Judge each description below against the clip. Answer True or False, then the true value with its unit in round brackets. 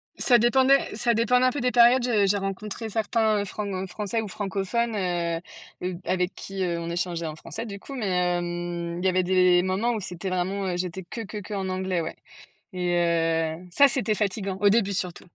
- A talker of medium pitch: False (195 Hz)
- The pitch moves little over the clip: False (3.7 semitones)